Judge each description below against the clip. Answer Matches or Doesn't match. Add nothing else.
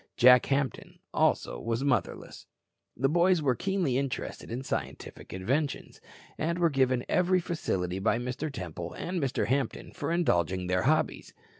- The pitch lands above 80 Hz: Matches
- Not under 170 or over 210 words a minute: Doesn't match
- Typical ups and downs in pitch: Doesn't match